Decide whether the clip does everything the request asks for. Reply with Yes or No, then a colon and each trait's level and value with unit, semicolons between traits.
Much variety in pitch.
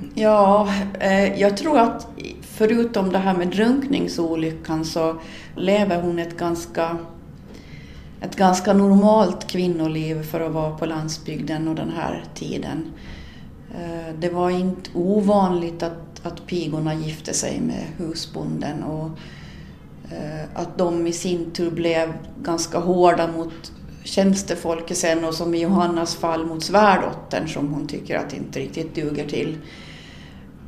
No: average, 2.7 semitones